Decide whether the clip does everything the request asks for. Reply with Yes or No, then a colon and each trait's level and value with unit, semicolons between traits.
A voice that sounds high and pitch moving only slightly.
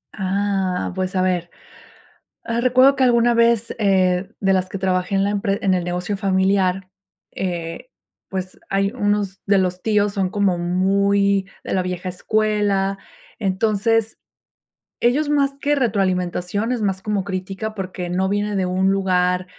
Yes: high, 195 Hz; narrow, 2.2 semitones